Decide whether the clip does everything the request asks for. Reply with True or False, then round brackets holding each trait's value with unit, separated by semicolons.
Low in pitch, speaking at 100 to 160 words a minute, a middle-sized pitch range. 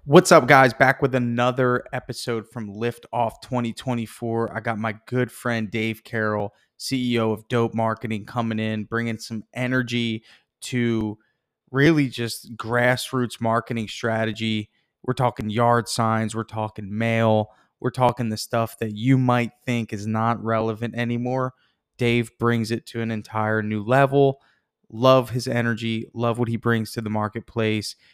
False (115 Hz; 150 wpm; 1.8 semitones)